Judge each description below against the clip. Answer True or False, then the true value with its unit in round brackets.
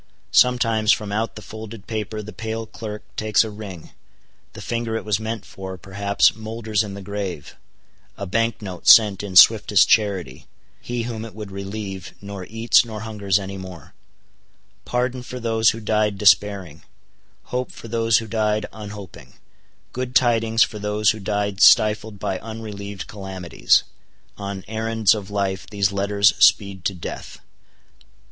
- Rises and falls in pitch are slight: True (2.1 semitones)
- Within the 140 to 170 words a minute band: True (150 wpm)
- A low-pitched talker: True (105 Hz)